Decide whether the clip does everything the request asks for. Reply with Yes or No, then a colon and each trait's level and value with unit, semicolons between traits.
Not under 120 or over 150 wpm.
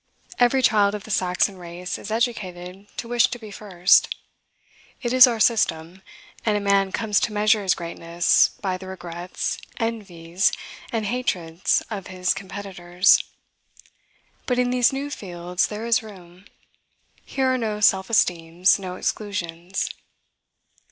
Yes: average, 140 wpm